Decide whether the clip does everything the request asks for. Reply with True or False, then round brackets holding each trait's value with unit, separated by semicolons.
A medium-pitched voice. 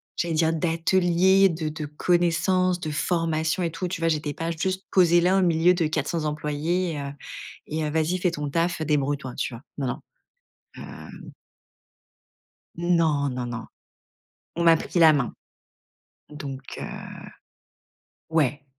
True (160 Hz)